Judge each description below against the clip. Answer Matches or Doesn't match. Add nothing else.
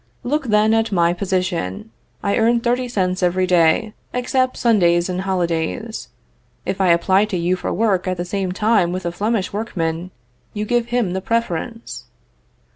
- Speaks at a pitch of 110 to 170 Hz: Doesn't match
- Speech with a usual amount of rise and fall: Matches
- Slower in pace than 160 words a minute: Doesn't match